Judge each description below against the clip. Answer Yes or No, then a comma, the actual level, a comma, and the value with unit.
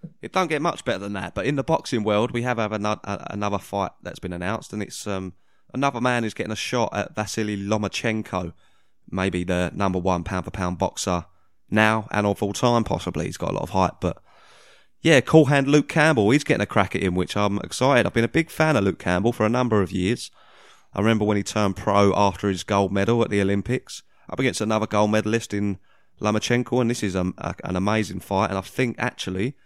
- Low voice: Yes, low, 105 Hz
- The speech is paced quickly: Yes, fast, 225 wpm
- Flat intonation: No, average, 3.7 semitones